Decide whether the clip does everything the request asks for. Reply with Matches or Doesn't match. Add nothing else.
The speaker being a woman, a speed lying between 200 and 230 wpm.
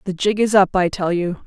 Doesn't match